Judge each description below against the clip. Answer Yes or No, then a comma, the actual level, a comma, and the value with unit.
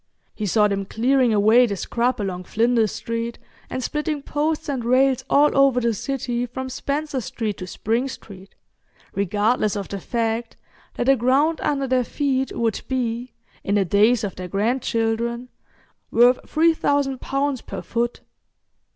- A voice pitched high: Yes, high, 240 Hz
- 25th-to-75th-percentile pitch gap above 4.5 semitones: No, average, 3.6 semitones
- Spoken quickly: No, average, 150 wpm